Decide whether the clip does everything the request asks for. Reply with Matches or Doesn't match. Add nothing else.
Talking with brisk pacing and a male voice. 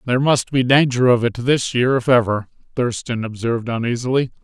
Doesn't match